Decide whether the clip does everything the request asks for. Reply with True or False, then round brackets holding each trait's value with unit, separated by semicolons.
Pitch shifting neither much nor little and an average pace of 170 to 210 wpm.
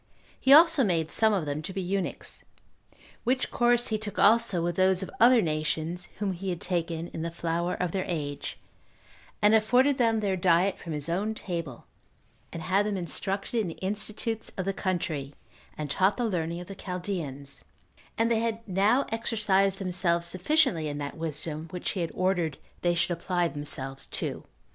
True (4.0 semitones; 180 wpm)